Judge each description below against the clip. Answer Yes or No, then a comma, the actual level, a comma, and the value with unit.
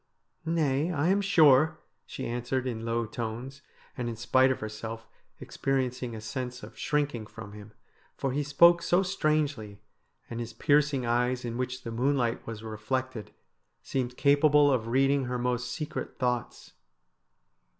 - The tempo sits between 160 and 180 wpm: No, average, 150 wpm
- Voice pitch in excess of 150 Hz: No, low, 125 Hz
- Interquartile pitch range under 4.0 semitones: Yes, average, 3.5 semitones